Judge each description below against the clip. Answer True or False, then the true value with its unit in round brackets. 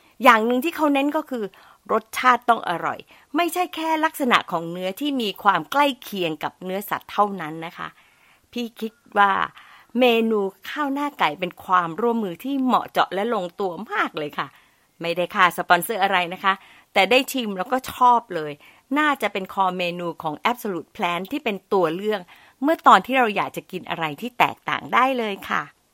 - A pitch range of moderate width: False (5.9 semitones)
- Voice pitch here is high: True (210 Hz)